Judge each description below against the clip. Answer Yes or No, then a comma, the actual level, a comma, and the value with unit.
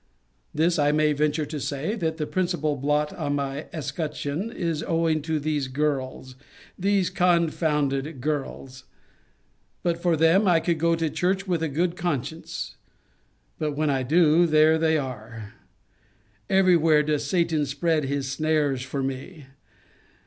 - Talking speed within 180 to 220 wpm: No, average, 145 wpm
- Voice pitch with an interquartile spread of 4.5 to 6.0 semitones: No, average, 2.9 semitones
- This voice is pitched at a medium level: Yes, medium, 155 Hz